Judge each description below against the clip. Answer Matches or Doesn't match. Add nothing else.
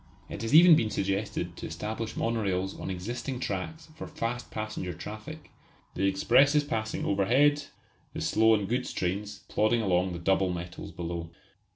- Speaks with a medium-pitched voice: Doesn't match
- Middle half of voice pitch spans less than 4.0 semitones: Doesn't match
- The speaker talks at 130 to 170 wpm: Matches